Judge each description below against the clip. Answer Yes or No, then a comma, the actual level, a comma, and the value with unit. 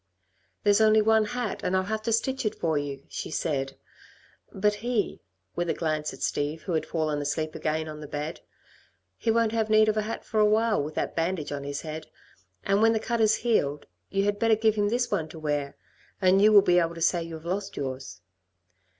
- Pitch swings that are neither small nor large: No, wide, 5.8 semitones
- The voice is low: No, medium, 185 Hz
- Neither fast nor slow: No, fast, 220 wpm